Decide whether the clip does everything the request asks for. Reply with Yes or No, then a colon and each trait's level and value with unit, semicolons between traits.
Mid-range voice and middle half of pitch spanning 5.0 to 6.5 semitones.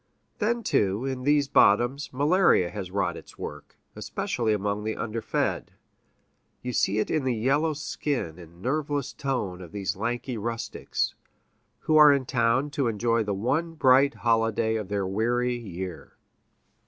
No: low, 115 Hz; average, 5.3 semitones